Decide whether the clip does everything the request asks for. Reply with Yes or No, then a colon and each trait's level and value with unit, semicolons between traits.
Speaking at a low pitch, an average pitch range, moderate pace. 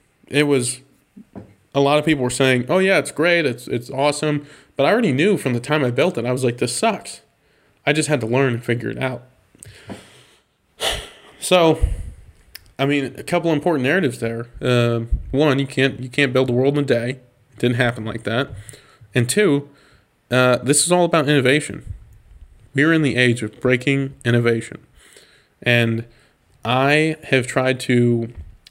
Yes: low, 130 Hz; average, 3.4 semitones; average, 175 wpm